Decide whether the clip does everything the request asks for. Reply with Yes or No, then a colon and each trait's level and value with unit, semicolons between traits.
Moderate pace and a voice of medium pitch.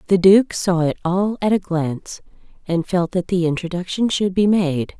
Yes: average, 190 wpm; medium, 180 Hz